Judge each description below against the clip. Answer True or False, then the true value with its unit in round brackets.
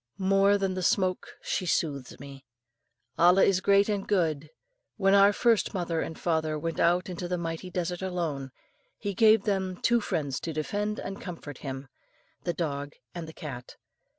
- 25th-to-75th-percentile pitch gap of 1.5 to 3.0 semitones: False (3.8 semitones)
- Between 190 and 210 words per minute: False (170 wpm)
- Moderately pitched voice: True (175 Hz)